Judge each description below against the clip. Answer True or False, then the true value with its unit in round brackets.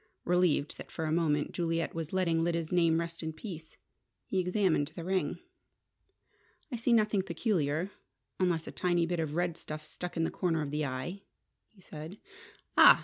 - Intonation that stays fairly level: True (2.3 semitones)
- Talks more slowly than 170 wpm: False (175 wpm)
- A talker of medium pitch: True (170 Hz)